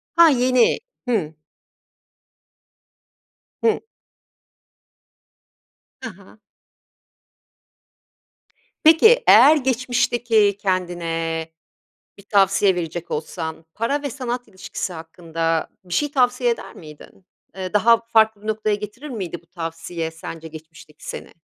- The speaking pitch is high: Yes, high, 200 Hz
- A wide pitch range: Yes, wide, 6.7 semitones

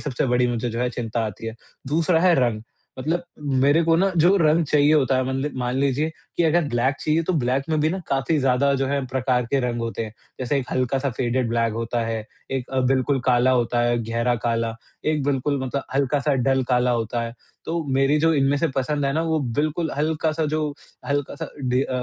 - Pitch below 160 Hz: Yes, low, 135 Hz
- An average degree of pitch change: Yes, average, 3.5 semitones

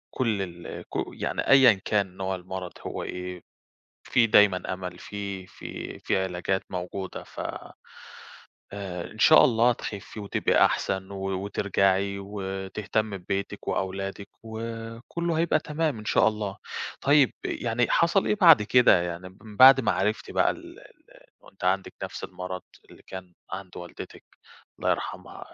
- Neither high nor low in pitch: No, low, 100 Hz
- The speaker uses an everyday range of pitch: Yes, average, 3.3 semitones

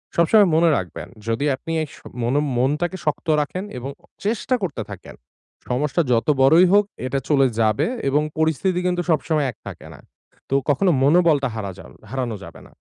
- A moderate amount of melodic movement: Yes, average, 4.8 semitones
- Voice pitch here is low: No, medium, 150 Hz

